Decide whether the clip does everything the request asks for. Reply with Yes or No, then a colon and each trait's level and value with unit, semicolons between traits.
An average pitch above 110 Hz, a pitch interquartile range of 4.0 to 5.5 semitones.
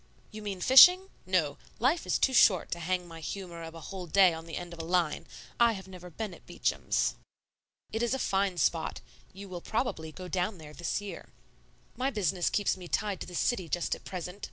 No: medium, 185 Hz; average, 3.2 semitones